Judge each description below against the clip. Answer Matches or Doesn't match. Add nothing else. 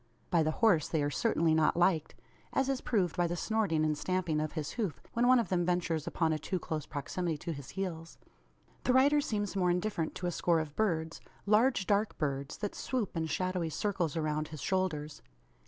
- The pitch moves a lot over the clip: Doesn't match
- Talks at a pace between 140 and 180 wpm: Doesn't match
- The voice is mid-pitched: Matches